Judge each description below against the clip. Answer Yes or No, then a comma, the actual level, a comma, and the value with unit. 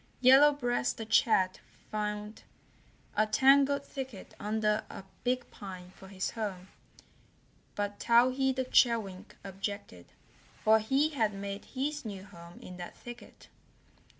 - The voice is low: No, high, 215 Hz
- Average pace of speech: No, slow, 125 wpm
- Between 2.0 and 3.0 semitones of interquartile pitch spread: No, average, 4.5 semitones